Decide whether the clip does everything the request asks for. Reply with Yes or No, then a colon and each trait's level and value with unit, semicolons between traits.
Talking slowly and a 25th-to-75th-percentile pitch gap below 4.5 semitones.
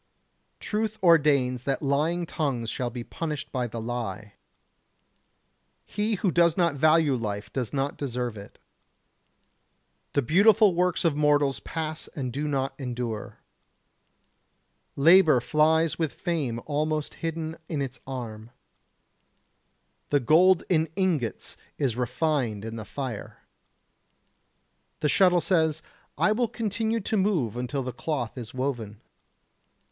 No: slow, 125 wpm; average, 5.2 semitones